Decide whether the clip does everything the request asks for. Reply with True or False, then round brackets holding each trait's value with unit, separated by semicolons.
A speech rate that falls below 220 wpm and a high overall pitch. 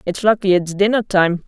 True (205 wpm; 195 Hz)